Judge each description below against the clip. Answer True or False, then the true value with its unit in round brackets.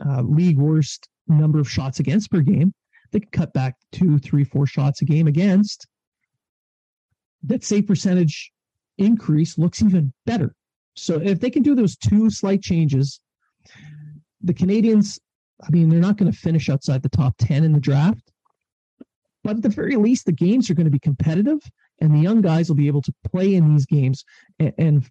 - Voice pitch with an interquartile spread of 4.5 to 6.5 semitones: True (5.0 semitones)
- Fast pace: False (185 wpm)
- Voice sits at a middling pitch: True (160 Hz)